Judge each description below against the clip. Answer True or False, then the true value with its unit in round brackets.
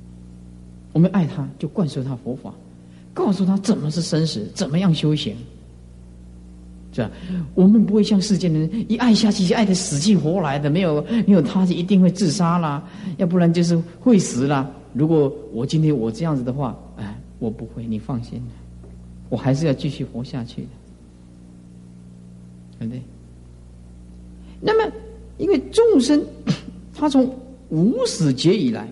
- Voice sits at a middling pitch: True (145 Hz)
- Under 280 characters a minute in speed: True (230 characters per minute)